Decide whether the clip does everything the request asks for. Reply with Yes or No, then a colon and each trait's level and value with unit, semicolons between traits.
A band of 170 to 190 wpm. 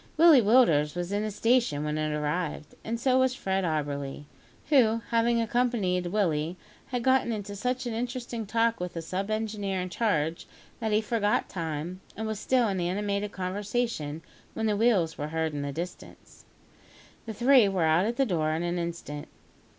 Yes: average, 180 wpm